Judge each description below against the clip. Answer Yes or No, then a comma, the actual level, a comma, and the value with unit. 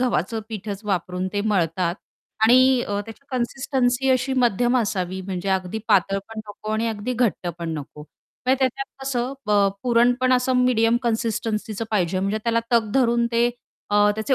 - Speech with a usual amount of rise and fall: Yes, average, 4.0 semitones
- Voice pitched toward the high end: Yes, high, 225 Hz